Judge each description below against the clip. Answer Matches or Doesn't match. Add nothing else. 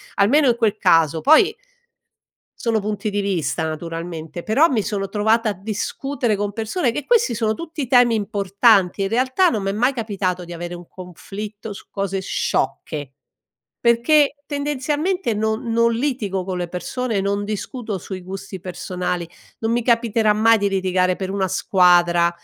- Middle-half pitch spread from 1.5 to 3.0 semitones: Doesn't match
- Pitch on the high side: Matches